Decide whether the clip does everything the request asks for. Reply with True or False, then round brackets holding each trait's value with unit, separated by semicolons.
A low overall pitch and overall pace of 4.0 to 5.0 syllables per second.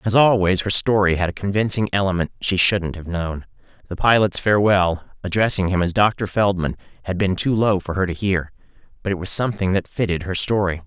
False (95 Hz; 5.7 syllables/s)